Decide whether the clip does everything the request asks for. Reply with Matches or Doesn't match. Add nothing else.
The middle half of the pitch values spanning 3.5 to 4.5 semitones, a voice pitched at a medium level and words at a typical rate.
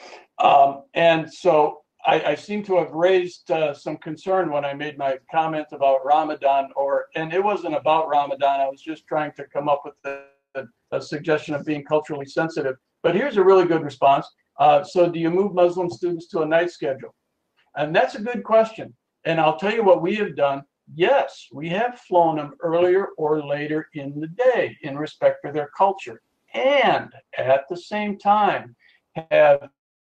Matches